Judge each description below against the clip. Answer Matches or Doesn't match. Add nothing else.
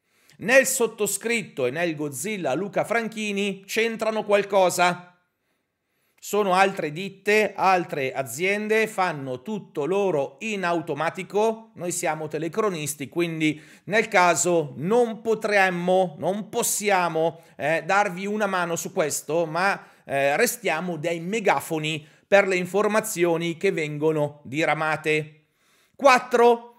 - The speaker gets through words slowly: Matches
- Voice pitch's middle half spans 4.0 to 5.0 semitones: Matches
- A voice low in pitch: Doesn't match